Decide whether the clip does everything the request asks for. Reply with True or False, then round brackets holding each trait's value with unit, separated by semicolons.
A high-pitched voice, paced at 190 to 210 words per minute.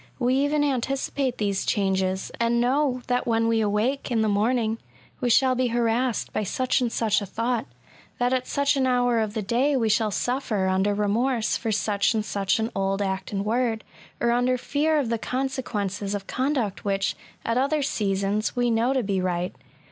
True (230 Hz; 195 wpm)